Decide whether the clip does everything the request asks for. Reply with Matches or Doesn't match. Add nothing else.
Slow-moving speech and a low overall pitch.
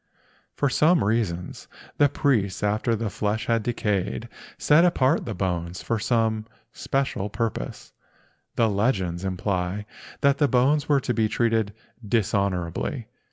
Matches